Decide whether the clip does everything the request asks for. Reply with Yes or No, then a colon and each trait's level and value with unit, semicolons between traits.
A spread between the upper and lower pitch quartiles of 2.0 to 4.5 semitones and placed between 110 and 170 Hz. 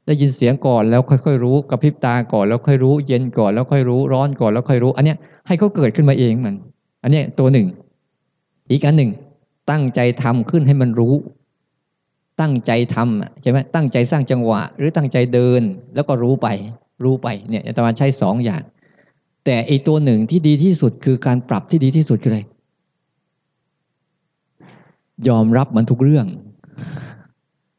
Yes: average, 3.8 semitones; low, 135 Hz